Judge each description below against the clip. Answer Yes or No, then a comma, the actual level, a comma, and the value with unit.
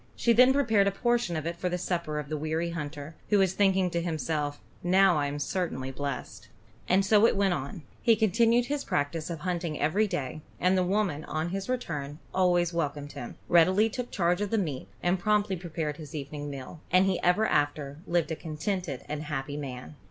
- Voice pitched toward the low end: No, medium, 170 Hz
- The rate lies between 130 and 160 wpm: No, fast, 205 wpm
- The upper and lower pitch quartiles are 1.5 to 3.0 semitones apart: No, average, 4.5 semitones